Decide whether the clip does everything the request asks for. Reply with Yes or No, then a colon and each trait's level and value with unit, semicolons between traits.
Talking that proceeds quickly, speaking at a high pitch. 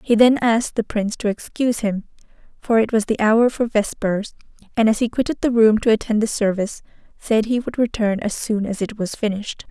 Yes: fast, 215 wpm; high, 220 Hz